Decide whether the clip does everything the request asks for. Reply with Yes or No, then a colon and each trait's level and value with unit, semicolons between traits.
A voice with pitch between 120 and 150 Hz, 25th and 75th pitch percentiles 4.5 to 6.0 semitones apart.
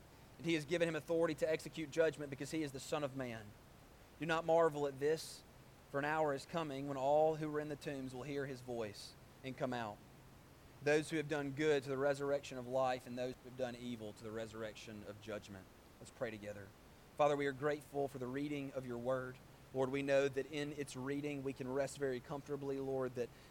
No: medium, 140 Hz; average, 2.8 semitones